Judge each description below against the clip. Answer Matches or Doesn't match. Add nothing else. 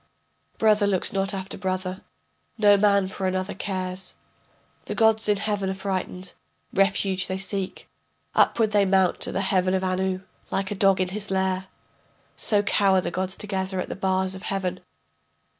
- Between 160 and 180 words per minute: Matches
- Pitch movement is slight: Matches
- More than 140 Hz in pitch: Matches